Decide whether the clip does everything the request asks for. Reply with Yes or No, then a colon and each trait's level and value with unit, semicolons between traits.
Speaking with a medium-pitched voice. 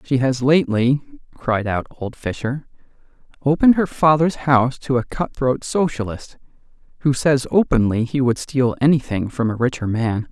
No: low, 130 Hz